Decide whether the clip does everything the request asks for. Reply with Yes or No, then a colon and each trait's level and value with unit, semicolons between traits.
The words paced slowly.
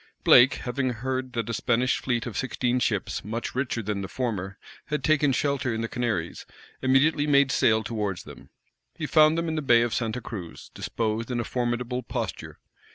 No: average, 185 wpm